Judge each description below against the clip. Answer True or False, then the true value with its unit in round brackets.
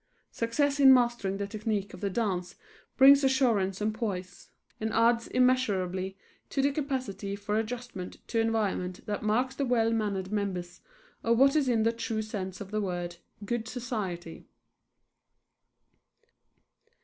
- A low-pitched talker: False (220 Hz)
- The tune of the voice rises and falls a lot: False (4.0 semitones)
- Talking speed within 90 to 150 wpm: True (140 wpm)